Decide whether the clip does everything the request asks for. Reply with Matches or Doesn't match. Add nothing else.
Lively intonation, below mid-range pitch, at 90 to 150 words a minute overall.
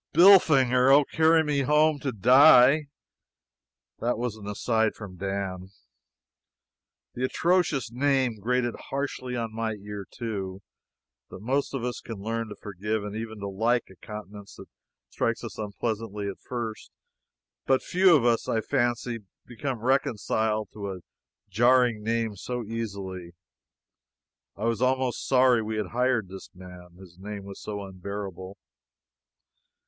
Doesn't match